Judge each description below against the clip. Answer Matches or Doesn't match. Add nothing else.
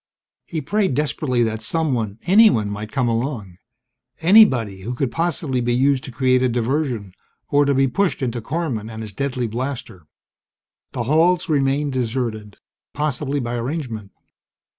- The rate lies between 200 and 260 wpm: Doesn't match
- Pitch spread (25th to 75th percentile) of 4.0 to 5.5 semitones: Matches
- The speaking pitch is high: Doesn't match